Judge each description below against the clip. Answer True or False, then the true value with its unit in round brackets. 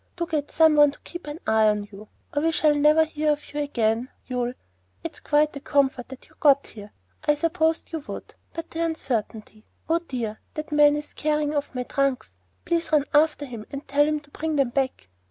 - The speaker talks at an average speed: False (220 wpm)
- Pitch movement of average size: True (3.5 semitones)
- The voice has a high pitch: True (290 Hz)